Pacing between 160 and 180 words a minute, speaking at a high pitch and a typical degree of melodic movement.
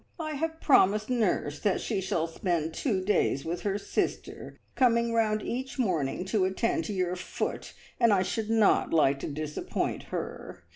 Yes: average, 165 wpm; high, 200 Hz; average, 4.9 semitones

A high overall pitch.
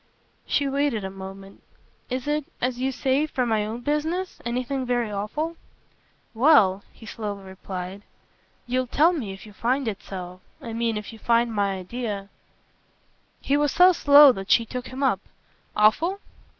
Yes: high, 235 Hz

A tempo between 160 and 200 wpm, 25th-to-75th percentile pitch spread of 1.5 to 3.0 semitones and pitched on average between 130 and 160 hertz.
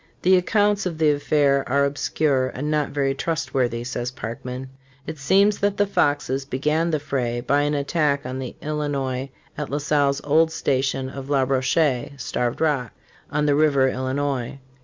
Yes: average, 165 wpm; narrow, 2.6 semitones; medium, 140 Hz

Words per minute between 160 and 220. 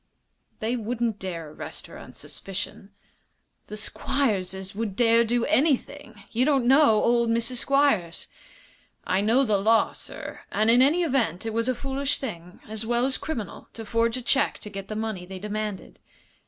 Yes: average, 170 wpm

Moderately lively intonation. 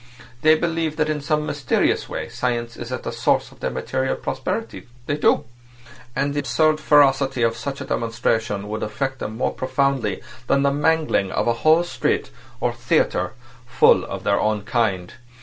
Yes: average, 4.2 semitones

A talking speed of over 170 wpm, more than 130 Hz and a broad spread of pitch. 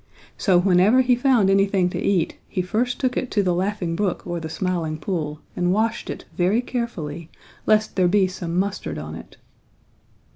No: average, 180 wpm; high, 190 Hz; average, 3.5 semitones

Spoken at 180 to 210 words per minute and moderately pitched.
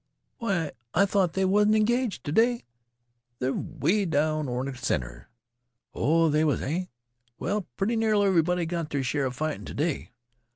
No: average, 170 wpm; medium, 165 Hz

